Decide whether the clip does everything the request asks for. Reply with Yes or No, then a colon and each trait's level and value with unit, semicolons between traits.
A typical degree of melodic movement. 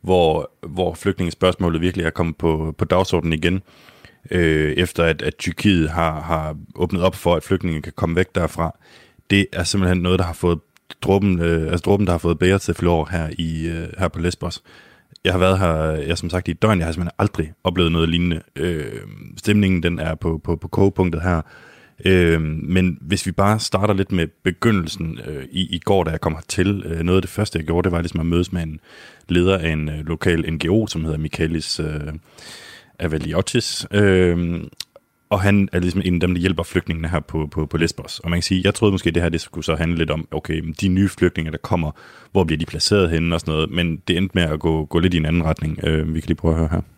No: narrow, 2.3 semitones